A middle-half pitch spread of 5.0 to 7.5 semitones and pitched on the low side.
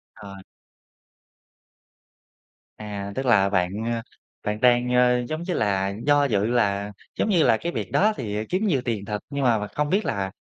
Yes: wide, 5.5 semitones; low, 115 Hz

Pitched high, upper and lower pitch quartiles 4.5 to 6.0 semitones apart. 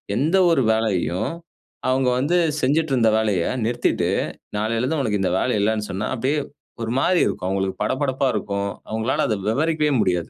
No: low, 115 Hz; average, 4.8 semitones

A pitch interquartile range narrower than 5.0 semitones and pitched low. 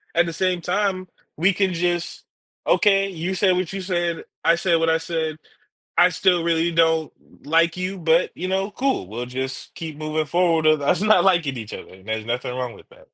No: average, 2.9 semitones; medium, 170 Hz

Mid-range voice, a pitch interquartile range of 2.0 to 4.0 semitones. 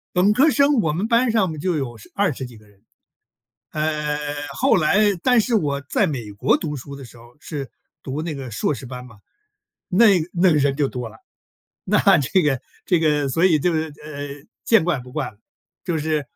No: medium, 150 Hz; average, 5.1 semitones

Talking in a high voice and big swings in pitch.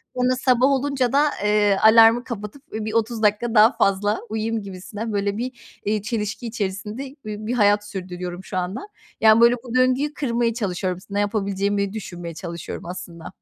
No: high, 215 Hz; average, 3.1 semitones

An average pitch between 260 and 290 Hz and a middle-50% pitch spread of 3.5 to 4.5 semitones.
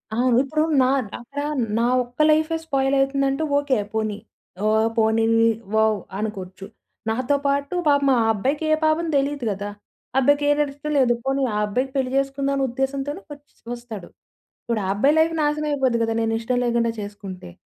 Yes: very high, 270 Hz; average, 4.2 semitones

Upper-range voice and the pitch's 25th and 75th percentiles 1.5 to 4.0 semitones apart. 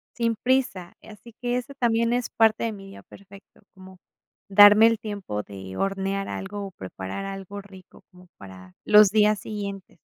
Yes: high, 200 Hz; average, 2.7 semitones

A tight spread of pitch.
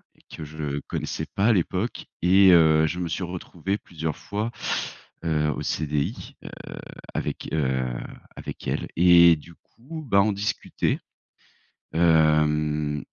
No: average, 3.6 semitones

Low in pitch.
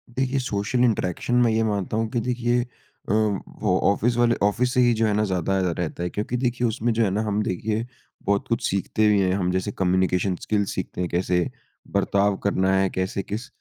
Yes: low, 105 Hz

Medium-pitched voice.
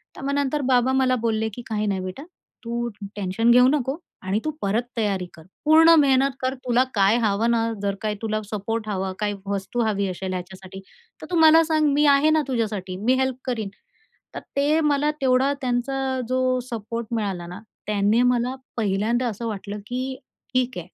No: high, 235 Hz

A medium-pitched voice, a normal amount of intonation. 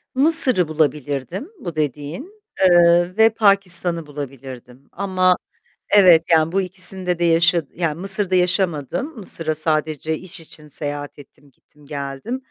Yes: medium, 170 Hz; average, 4.0 semitones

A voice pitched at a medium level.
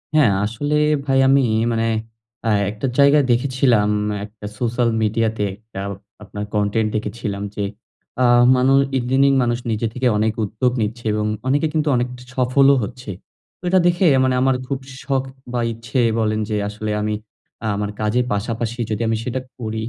No: low, 120 Hz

